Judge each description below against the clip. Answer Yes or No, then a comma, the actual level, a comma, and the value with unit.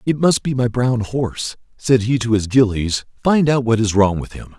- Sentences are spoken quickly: Yes, fast, 235 wpm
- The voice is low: Yes, low, 120 Hz